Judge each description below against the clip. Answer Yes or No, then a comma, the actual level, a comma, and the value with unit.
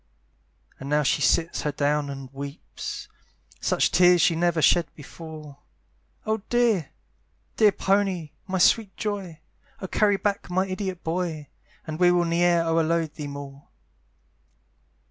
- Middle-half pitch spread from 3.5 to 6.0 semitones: Yes, average, 3.9 semitones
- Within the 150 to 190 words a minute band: No, slow, 135 wpm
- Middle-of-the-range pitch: Yes, medium, 170 Hz